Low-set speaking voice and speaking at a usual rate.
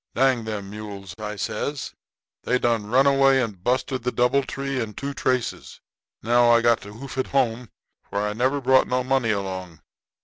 Yes: low, 120 Hz; average, 175 wpm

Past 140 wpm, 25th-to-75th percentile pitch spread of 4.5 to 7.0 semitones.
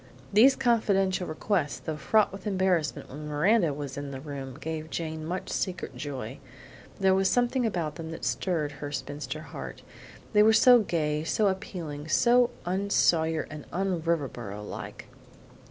Yes: average, 155 wpm; average, 4.8 semitones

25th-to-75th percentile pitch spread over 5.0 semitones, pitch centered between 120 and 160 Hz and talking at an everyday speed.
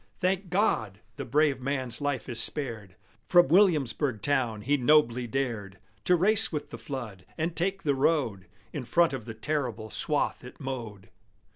Yes: wide, 5.4 semitones; low, 135 Hz; average, 160 wpm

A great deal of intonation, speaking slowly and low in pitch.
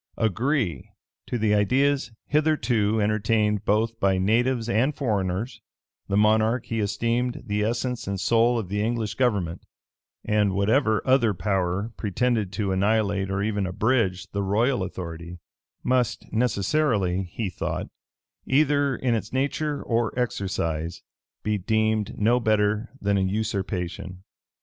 No: average, 3.5 semitones; slow, 130 wpm; low, 110 Hz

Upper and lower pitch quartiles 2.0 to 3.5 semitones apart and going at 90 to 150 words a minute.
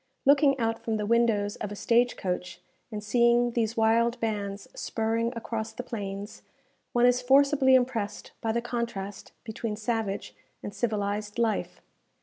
Yes: narrow, 2.5 semitones; average, 145 wpm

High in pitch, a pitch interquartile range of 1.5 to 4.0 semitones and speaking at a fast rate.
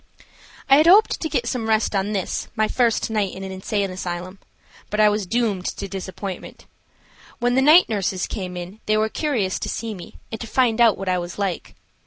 Yes: high, 210 Hz; average, 3.6 semitones; fast, 210 wpm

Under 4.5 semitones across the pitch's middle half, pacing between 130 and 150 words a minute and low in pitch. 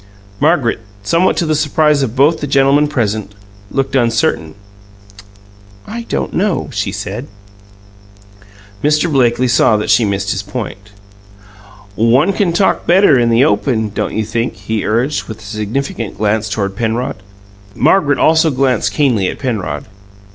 No: wide, 5.4 semitones; average, 145 wpm; low, 125 Hz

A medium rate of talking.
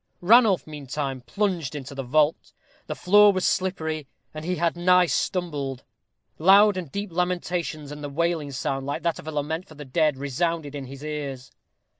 Yes: average, 175 wpm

